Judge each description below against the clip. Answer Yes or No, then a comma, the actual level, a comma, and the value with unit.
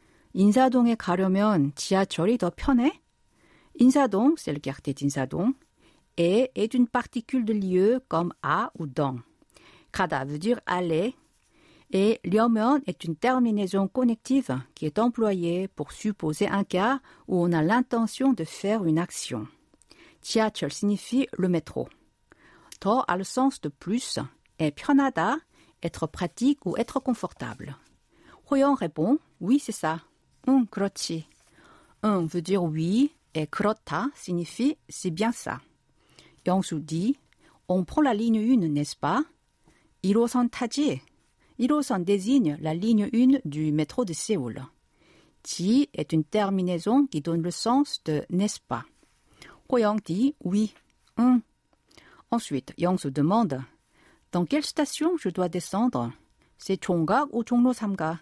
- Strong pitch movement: Yes, wide, 6.7 semitones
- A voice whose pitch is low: No, high, 205 Hz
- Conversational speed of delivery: No, slow, 135 wpm